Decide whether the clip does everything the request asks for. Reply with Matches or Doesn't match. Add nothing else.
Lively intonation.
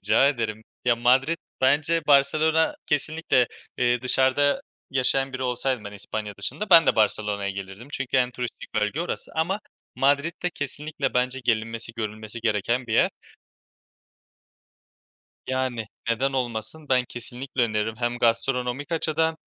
Doesn't match